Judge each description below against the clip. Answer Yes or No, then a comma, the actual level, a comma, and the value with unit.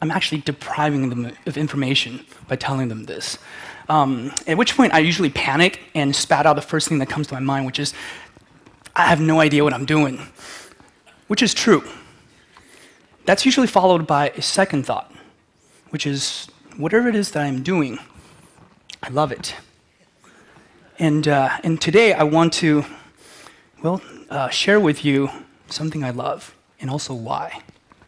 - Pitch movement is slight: No, average, 3.1 semitones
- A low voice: No, medium, 150 Hz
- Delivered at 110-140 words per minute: No, fast, 160 wpm